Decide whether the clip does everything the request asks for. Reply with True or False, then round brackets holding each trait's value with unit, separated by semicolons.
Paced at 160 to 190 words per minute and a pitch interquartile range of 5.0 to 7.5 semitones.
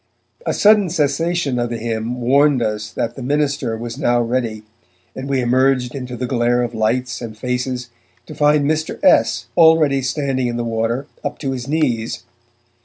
False (175 wpm; 3.0 semitones)